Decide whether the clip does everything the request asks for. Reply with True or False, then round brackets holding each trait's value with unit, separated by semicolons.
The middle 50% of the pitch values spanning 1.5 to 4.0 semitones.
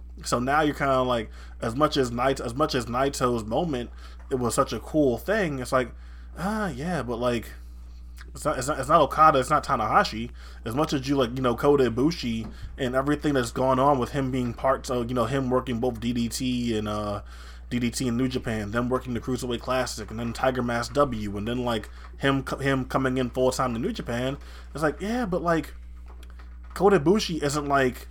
True (3.6 semitones)